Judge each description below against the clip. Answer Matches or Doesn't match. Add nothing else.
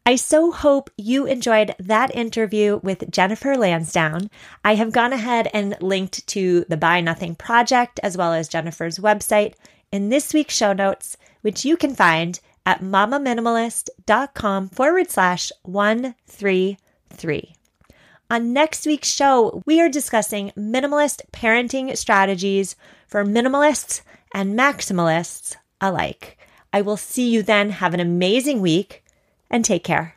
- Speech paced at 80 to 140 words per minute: Matches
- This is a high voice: Matches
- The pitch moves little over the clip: Doesn't match